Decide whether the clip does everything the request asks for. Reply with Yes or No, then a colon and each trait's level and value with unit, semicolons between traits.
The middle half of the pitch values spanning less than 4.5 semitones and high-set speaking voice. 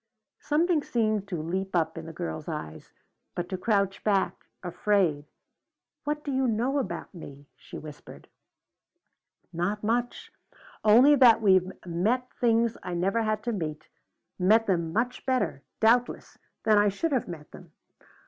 No: average, 5.3 semitones; high, 205 Hz